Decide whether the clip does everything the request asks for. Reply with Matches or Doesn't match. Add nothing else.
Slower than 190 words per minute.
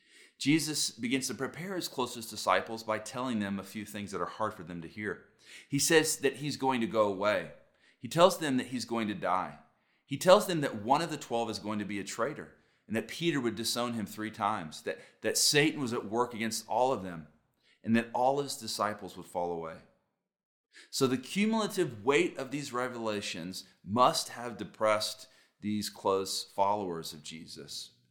Doesn't match